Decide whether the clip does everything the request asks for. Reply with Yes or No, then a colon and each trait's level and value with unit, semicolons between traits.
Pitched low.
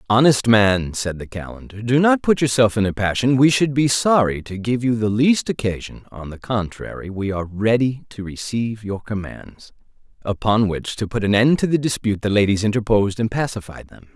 Yes: low, 110 Hz